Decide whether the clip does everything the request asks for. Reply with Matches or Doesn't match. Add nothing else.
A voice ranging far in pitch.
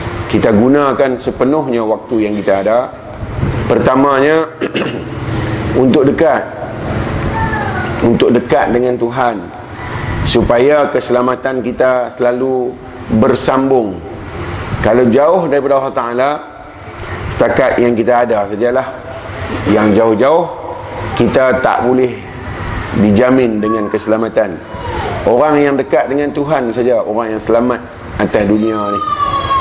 Doesn't match